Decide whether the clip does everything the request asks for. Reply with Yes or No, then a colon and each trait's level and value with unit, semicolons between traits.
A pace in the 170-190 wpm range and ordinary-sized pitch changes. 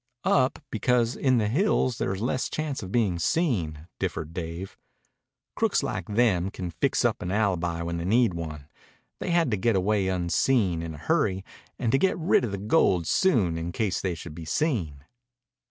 No: average, 185 wpm; wide, 6.2 semitones